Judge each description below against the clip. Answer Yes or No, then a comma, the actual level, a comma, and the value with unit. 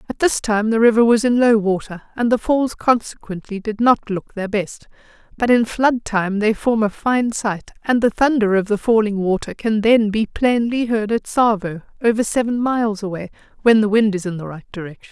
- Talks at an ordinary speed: No, fast, 210 wpm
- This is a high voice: Yes, high, 220 Hz